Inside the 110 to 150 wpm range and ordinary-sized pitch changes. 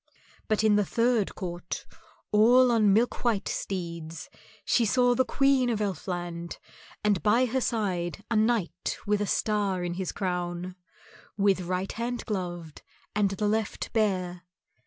Yes: average, 145 wpm; average, 4.1 semitones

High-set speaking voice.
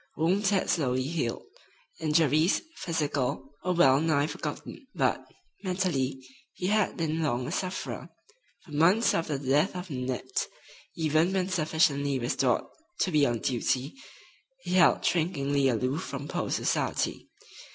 No: medium, 155 Hz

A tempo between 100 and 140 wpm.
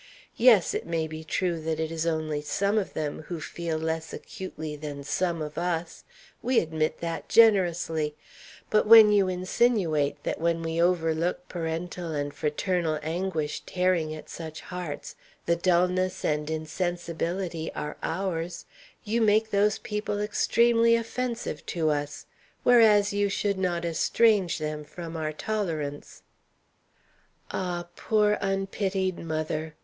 Yes: slow, 135 wpm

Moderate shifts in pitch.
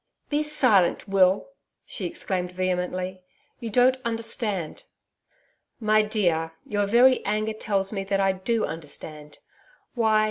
Yes: average, 3.6 semitones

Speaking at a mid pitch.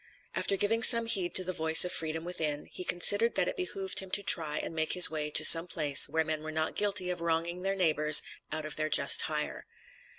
Yes: medium, 165 Hz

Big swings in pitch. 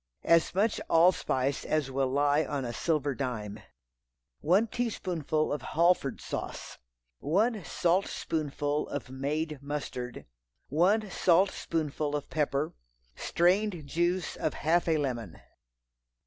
No: average, 3.9 semitones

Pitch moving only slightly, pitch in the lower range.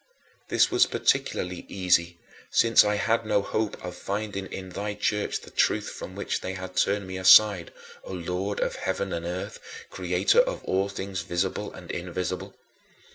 Yes: narrow, 2.3 semitones; very low, 95 Hz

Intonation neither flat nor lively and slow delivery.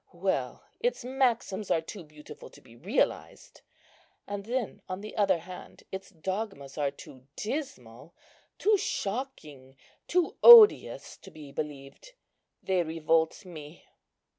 No: wide, 7.1 semitones; slow, 125 wpm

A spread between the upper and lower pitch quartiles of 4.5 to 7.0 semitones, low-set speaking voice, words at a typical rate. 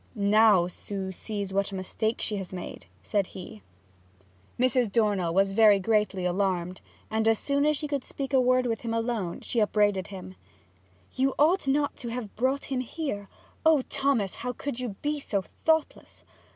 No: average, 4.9 semitones; high, 220 Hz; average, 175 wpm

